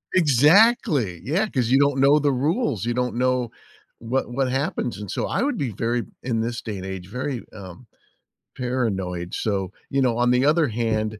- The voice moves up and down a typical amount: Yes, average, 4.1 semitones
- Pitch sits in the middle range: No, low, 125 Hz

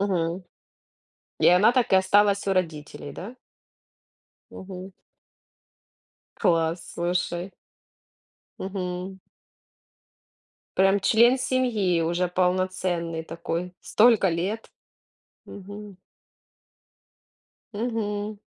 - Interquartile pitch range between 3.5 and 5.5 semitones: No, average, 2.8 semitones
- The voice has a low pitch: No, high, 190 Hz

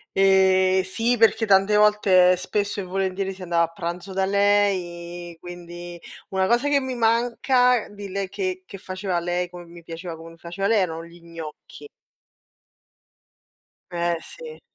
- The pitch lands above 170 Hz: Yes, high, 190 Hz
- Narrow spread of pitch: No, average, 3.0 semitones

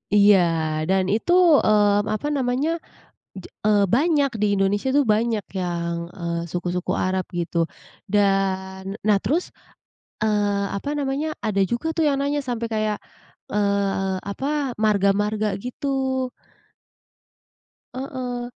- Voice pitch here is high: Yes, high, 210 Hz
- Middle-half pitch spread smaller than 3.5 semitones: No, average, 4.6 semitones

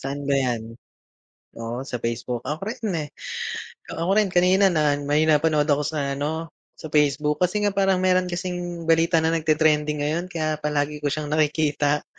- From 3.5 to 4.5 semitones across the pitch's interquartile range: No, average, 3.1 semitones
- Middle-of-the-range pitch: Yes, medium, 155 Hz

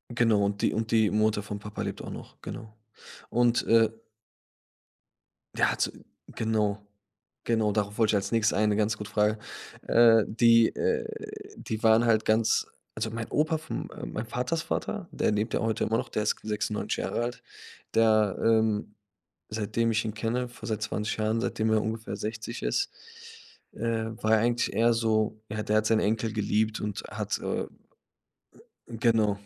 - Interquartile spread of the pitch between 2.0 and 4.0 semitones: No, narrow, 1.4 semitones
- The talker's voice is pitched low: Yes, low, 110 Hz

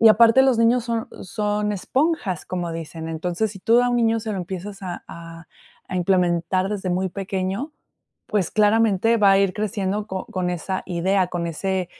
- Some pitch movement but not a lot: Yes, average, 3.6 semitones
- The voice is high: Yes, high, 195 Hz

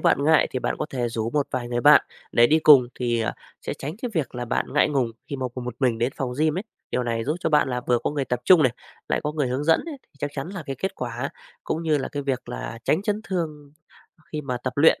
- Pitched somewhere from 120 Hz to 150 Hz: Yes, low, 135 Hz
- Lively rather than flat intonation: No, average, 3.8 semitones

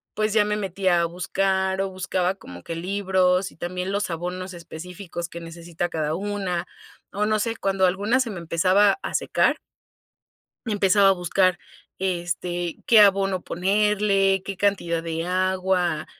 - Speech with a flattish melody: Yes, narrow, 2.3 semitones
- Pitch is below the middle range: No, medium, 185 Hz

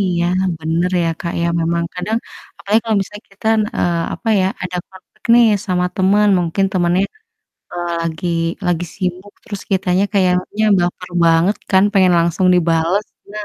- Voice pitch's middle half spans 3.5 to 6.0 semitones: No, narrow, 2.5 semitones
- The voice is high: No, medium, 180 Hz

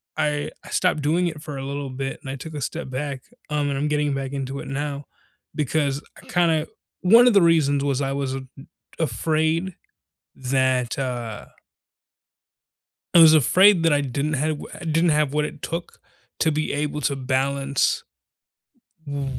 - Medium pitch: Yes, medium, 145 Hz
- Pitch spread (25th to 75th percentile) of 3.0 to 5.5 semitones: No, narrow, 2.5 semitones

